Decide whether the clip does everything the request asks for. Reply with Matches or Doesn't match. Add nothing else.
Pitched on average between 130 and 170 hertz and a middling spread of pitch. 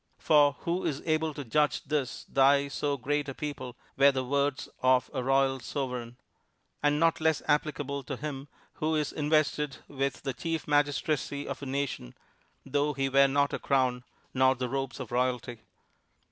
Doesn't match